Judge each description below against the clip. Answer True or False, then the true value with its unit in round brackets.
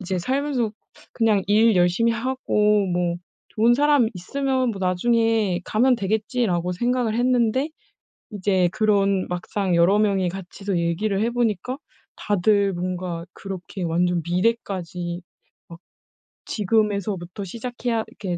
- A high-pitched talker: True (205 Hz)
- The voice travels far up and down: False (4.4 semitones)